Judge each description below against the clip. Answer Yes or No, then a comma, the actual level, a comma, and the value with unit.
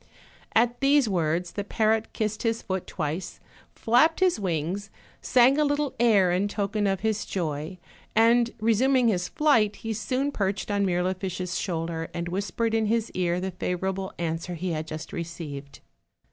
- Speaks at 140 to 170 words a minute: Yes, average, 165 wpm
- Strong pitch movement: No, average, 4.4 semitones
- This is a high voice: Yes, high, 195 Hz